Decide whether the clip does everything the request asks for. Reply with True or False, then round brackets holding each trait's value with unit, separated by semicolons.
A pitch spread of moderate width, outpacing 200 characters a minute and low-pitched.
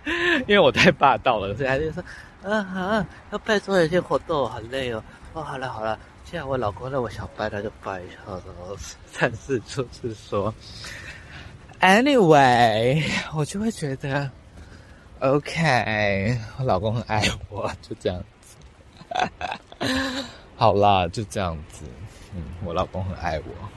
False (6.9 semitones; 225 characters per minute; 110 Hz)